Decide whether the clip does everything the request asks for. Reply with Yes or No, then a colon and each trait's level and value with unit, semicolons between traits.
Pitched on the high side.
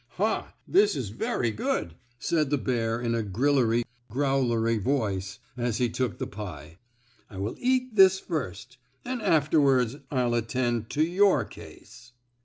No: low, 125 Hz